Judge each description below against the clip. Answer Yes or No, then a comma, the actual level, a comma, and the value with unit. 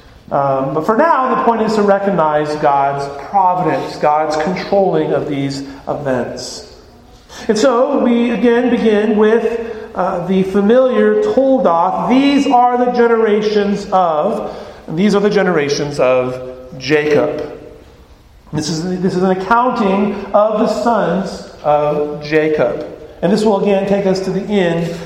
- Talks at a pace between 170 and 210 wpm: No, average, 140 wpm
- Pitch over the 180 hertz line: Yes, high, 190 Hz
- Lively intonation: Yes, wide, 6.6 semitones